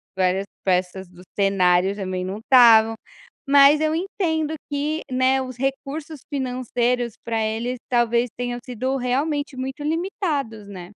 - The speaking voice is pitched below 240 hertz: No, very high, 250 Hz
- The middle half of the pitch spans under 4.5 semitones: No, average, 5.2 semitones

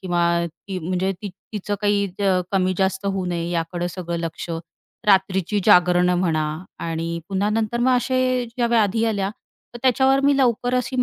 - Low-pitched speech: No, high, 190 Hz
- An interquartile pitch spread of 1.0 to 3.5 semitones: No, average, 4.2 semitones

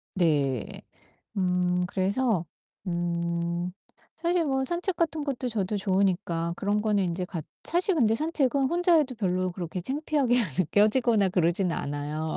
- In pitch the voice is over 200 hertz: No, high, 195 Hz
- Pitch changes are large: Yes, wide, 7.4 semitones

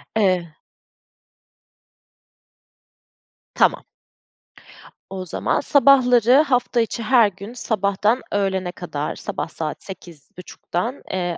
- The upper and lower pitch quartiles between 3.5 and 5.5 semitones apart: Yes, average, 5.1 semitones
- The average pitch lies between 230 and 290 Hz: No, high, 200 Hz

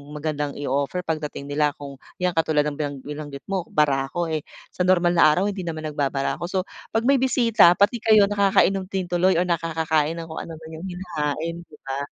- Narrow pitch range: No, average, 3.7 semitones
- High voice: No, medium, 165 Hz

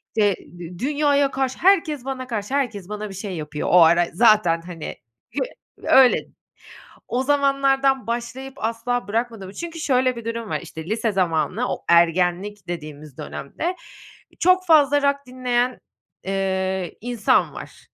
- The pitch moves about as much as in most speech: No, wide, 6.3 semitones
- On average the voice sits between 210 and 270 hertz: Yes, high, 230 Hz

